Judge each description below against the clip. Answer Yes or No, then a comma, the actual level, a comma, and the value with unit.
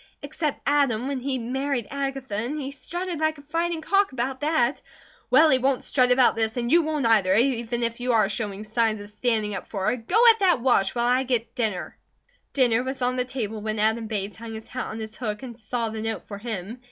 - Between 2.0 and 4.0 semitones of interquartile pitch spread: Yes, average, 3.7 semitones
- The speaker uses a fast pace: Yes, fast, 225 wpm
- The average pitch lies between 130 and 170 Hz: No, high, 245 Hz